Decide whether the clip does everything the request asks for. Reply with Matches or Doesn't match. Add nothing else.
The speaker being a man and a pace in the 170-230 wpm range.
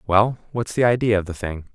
Doesn't match